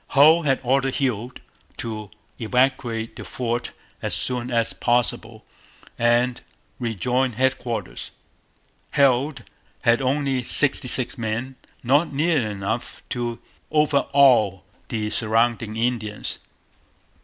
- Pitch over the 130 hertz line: No, low, 120 Hz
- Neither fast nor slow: No, slow, 100 wpm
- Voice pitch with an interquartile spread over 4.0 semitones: No, average, 2.7 semitones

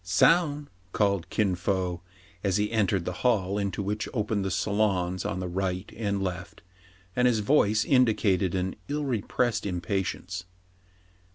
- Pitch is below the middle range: Yes, low, 100 Hz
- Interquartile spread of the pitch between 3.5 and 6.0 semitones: No, average, 2.9 semitones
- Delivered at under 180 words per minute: Yes, average, 155 wpm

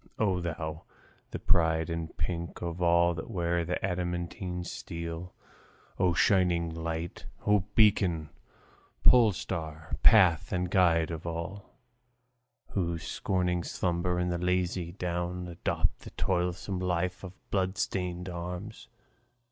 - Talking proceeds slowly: Yes, slow, 120 wpm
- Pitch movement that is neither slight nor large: No, narrow, 1.5 semitones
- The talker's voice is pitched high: No, very low, 90 Hz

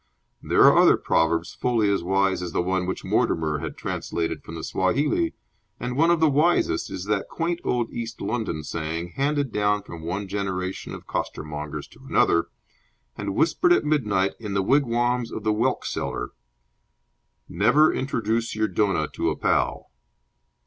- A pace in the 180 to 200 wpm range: No, average, 165 wpm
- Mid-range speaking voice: No, low, 105 Hz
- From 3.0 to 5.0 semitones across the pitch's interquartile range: No, wide, 5.5 semitones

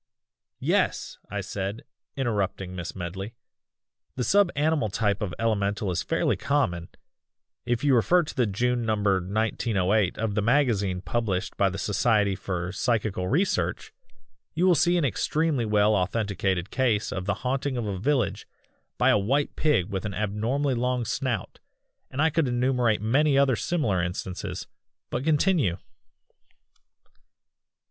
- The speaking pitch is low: Yes, low, 110 Hz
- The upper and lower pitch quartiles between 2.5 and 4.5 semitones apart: No, wide, 5.4 semitones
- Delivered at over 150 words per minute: No, average, 140 wpm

